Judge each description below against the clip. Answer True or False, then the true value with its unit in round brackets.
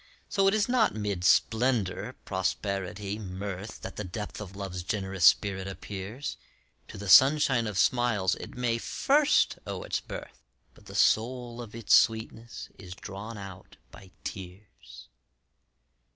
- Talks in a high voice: False (105 Hz)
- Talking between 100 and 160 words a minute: True (140 wpm)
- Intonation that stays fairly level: False (3.7 semitones)